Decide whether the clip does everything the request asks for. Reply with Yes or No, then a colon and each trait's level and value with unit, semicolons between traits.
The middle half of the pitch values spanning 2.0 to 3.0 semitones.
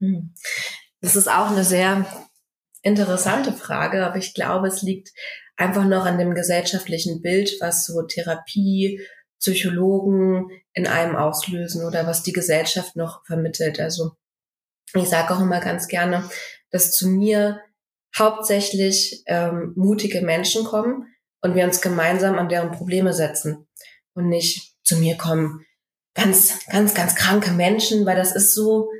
Yes: narrow, 2.4 semitones